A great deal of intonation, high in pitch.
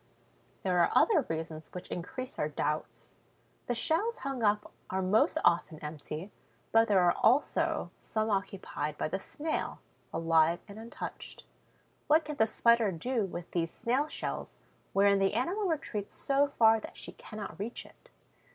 Yes: wide, 6.4 semitones; high, 205 Hz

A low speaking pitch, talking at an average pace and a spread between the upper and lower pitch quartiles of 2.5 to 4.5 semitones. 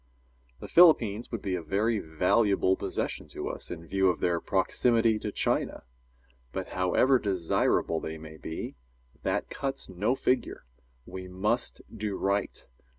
Yes: low, 100 Hz; average, 145 wpm; average, 4.1 semitones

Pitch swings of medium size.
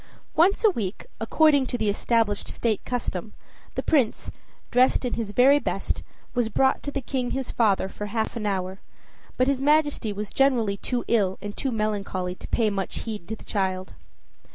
Yes: average, 4.4 semitones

